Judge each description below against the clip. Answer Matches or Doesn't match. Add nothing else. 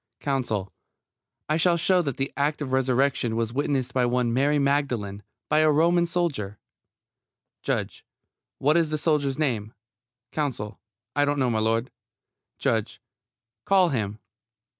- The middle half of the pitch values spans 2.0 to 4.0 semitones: Doesn't match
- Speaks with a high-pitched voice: Doesn't match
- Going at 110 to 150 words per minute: Matches